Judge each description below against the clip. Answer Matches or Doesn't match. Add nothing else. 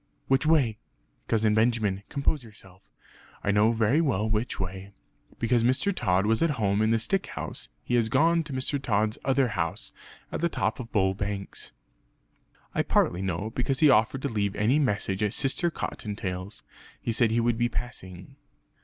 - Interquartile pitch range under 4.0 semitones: Doesn't match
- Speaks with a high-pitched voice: Doesn't match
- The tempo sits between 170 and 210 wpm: Matches